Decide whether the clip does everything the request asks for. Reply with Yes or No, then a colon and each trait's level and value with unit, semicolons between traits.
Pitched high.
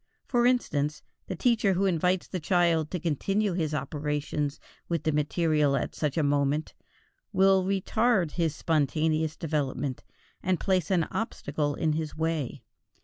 No: medium, 160 Hz